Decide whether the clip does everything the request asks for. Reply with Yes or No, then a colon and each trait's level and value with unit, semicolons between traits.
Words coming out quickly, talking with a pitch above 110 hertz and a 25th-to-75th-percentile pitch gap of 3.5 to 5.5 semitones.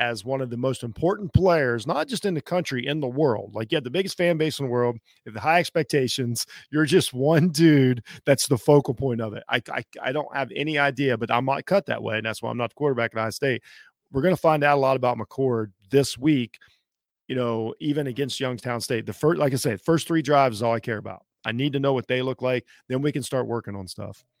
Yes: fast, 260 wpm; low, 135 Hz; average, 4.0 semitones